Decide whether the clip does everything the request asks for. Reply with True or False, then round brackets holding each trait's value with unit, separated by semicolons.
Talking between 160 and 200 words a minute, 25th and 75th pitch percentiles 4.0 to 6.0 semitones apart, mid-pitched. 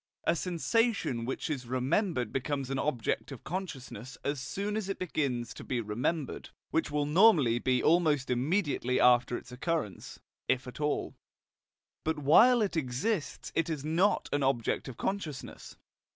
False (150 wpm; 5.2 semitones; 145 Hz)